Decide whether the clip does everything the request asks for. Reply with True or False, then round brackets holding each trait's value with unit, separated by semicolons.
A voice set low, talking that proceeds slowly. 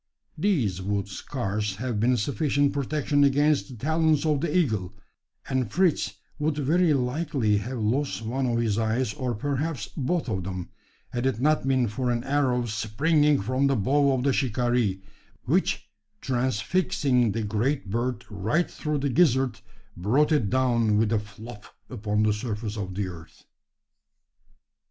False (125 Hz; 155 wpm)